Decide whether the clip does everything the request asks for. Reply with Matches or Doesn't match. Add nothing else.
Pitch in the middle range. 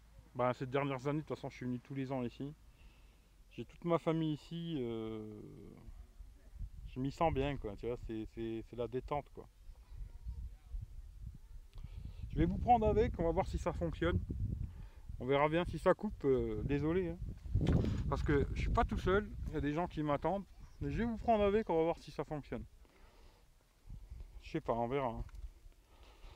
Doesn't match